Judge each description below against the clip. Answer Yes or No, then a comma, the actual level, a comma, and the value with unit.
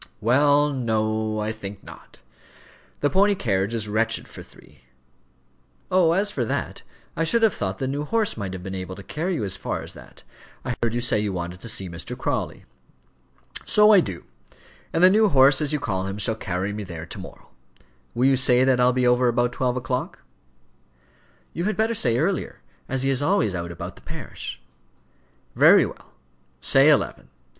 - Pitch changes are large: Yes, wide, 6.4 semitones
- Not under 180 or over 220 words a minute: Yes, average, 190 wpm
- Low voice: Yes, low, 120 Hz